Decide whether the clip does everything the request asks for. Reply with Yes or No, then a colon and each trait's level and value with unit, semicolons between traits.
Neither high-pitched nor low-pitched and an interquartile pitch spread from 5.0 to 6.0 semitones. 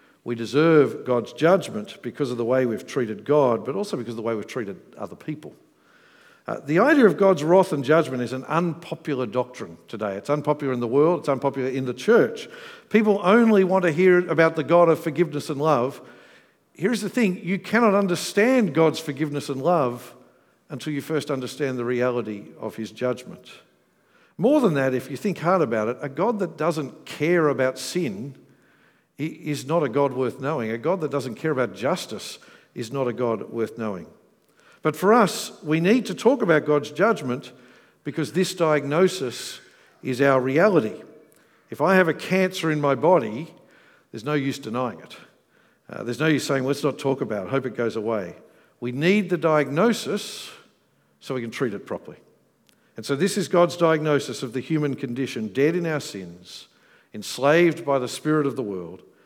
Yes: medium, 150 Hz; wide, 5.4 semitones